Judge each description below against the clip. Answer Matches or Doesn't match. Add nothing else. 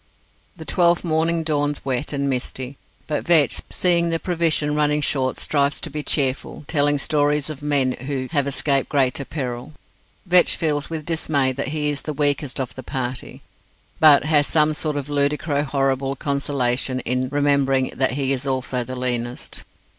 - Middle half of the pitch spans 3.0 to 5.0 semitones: Doesn't match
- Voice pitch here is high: Doesn't match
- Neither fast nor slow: Matches